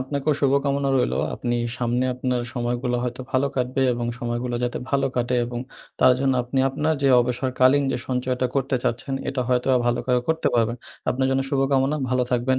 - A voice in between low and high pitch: No, low, 130 Hz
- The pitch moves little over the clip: Yes, narrow, 1.8 semitones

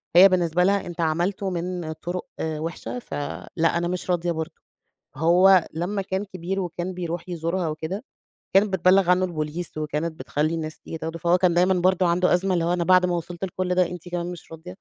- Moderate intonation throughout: No, narrow, 1.9 semitones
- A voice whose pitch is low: No, medium, 175 Hz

